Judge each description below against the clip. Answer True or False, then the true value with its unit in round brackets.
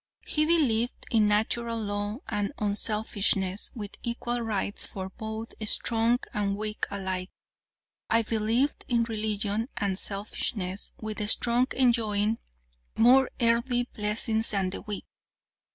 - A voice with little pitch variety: True (2.3 semitones)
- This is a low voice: False (220 Hz)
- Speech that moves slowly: True (120 wpm)